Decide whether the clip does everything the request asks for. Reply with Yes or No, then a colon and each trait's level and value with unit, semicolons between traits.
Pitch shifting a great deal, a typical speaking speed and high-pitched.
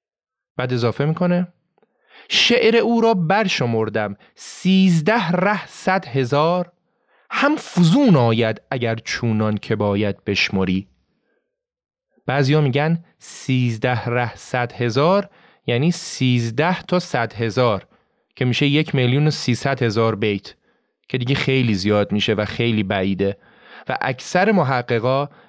No: wide, 7.7 semitones; average, 120 wpm; low, 135 Hz